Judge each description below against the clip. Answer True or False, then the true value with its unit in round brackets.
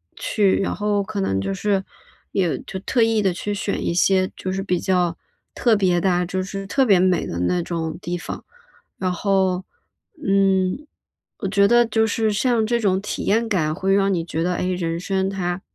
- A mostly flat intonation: True (2.3 semitones)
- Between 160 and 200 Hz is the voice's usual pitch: True (190 Hz)